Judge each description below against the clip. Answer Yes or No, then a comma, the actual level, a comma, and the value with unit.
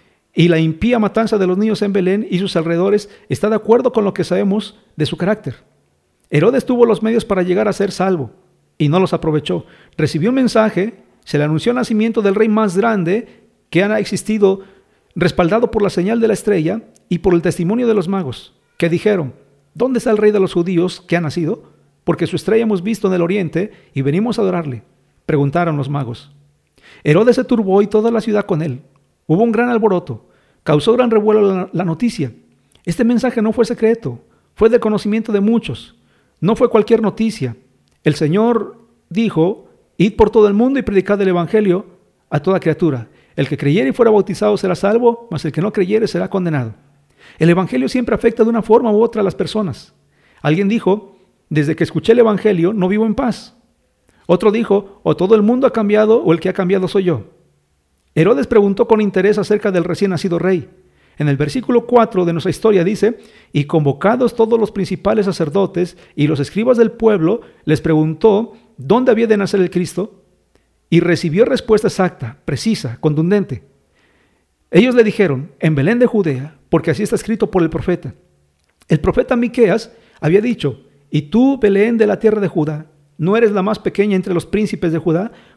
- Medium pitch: No, high, 195 Hz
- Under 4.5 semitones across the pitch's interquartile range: No, average, 4.9 semitones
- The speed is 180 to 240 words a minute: Yes, fast, 190 wpm